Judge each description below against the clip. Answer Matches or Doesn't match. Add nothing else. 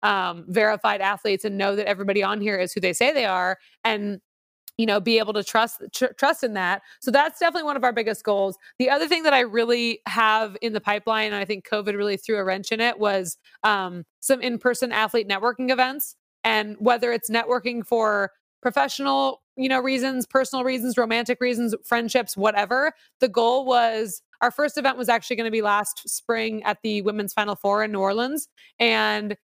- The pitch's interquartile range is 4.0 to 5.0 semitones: Doesn't match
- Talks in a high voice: Matches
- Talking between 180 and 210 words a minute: Matches